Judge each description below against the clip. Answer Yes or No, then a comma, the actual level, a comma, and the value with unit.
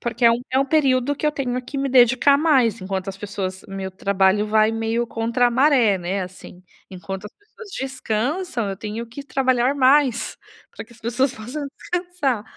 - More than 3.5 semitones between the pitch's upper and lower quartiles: Yes, average, 4.7 semitones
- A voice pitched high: Yes, high, 240 Hz